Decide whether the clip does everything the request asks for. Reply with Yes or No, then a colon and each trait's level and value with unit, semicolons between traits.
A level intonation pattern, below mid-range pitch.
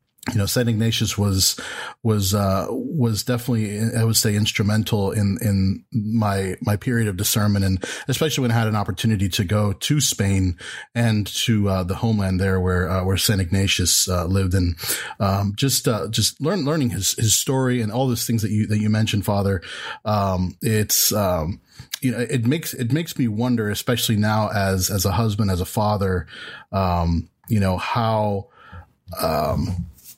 No: average, 3.2 semitones; low, 105 Hz